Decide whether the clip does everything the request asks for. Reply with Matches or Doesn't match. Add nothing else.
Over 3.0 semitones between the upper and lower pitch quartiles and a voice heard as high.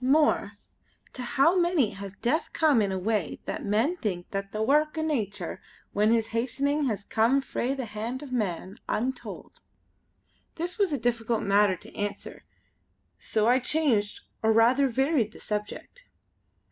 Matches